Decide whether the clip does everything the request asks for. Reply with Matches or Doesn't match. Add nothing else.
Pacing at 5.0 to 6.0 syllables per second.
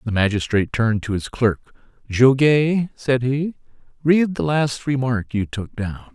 Doesn't match